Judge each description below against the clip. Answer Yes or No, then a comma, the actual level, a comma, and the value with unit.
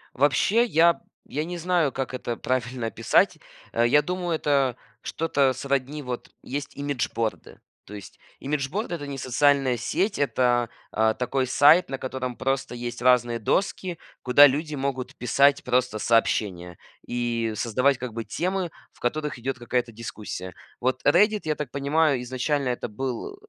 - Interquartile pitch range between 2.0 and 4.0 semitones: Yes, average, 3.4 semitones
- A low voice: Yes, low, 130 Hz